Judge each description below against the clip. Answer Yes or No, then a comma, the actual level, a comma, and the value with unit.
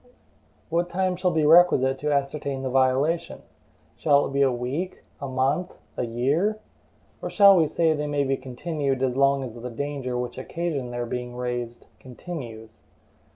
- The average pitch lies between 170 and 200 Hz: No, medium, 140 Hz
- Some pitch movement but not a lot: Yes, average, 4.4 semitones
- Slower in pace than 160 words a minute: No, average, 165 wpm